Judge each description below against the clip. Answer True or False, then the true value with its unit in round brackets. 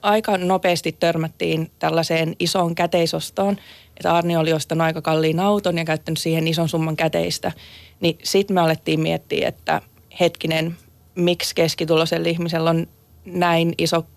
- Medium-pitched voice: True (165 Hz)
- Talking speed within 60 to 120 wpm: False (135 wpm)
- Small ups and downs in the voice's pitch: True (1.4 semitones)